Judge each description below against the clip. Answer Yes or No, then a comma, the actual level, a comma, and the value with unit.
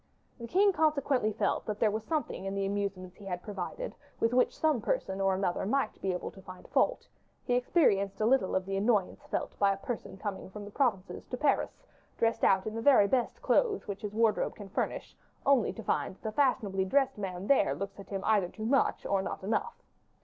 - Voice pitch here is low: No, high, 210 Hz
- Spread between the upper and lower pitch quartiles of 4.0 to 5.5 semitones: Yes, average, 4.5 semitones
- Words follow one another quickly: Yes, fast, 215 wpm